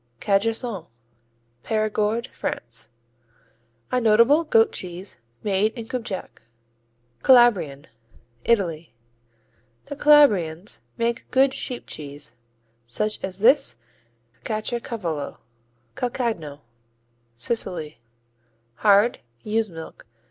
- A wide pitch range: Yes, wide, 6.0 semitones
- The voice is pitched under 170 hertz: No, high, 215 Hz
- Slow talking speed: Yes, slow, 85 wpm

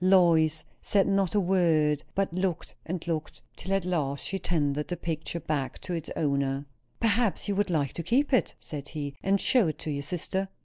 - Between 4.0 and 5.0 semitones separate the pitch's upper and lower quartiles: Yes, average, 4.3 semitones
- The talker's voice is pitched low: No, medium, 170 Hz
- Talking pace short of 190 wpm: No, average, 195 wpm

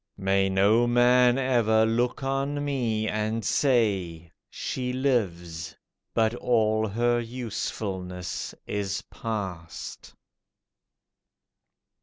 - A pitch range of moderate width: Yes, average, 4.0 semitones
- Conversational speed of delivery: No, slow, 85 wpm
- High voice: No, low, 110 Hz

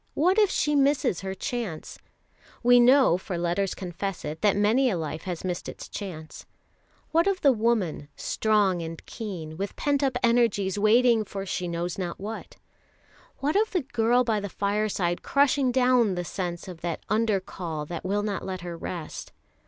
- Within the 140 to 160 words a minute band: No, average, 175 wpm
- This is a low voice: No, high, 205 Hz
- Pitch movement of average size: No, wide, 5.8 semitones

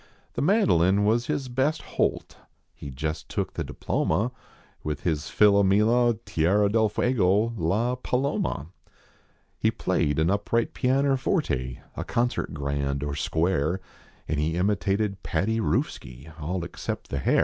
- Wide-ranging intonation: Yes, wide, 6.9 semitones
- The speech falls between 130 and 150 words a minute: Yes, slow, 135 wpm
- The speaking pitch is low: Yes, low, 100 Hz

